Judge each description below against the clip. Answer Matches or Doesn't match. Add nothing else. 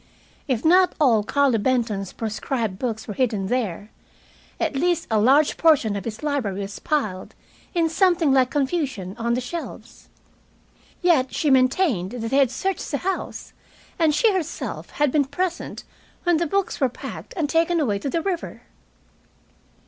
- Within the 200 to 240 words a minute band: Doesn't match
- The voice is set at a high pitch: Matches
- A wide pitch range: Matches